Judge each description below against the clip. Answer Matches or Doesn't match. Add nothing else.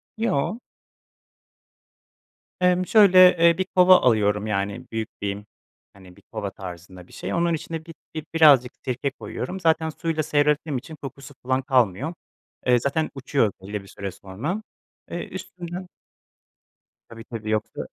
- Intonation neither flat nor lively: Doesn't match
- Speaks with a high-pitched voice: Doesn't match